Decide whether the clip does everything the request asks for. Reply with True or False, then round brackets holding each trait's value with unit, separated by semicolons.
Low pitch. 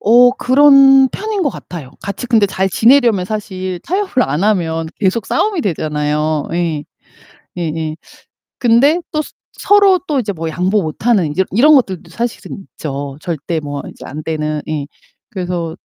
False (190 Hz)